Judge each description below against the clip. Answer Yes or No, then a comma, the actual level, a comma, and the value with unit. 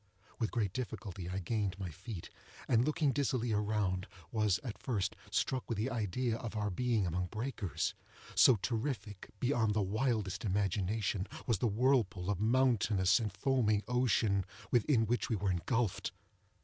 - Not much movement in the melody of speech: No, average, 3.7 semitones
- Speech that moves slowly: No, average, 150 wpm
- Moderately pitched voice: No, low, 110 Hz